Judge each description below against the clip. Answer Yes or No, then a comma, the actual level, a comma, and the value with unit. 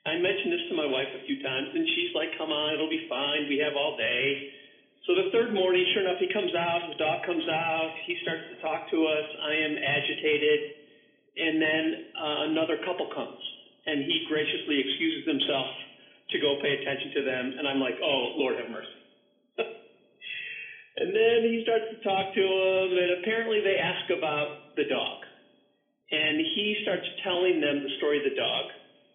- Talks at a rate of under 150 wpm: No, average, 180 wpm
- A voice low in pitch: No, medium, 180 Hz